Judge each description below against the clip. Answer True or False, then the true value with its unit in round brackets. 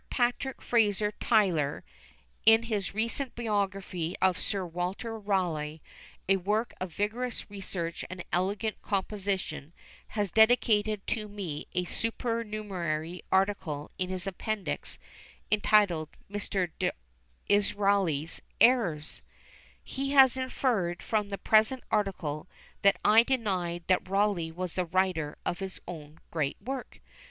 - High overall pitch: True (195 Hz)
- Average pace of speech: False (115 wpm)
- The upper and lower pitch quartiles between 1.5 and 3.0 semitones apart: False (3.8 semitones)